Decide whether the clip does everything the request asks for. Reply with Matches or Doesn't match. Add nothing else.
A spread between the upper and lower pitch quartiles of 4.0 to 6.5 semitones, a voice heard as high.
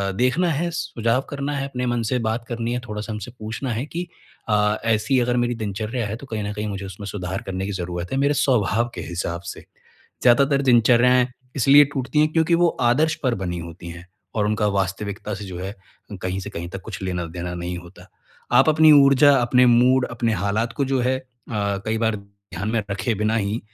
Doesn't match